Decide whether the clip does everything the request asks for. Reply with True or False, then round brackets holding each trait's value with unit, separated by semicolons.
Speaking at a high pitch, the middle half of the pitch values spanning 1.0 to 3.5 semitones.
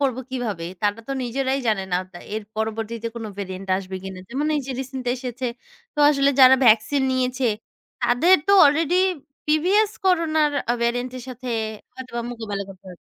False (250 Hz; 4.1 semitones)